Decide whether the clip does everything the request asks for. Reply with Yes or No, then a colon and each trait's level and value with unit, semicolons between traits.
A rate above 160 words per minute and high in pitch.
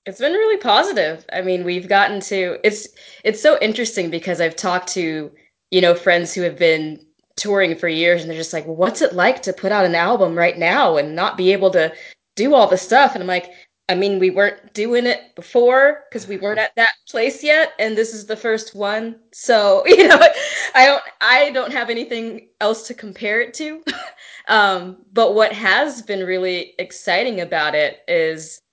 Yes: average, 200 wpm; high, 200 Hz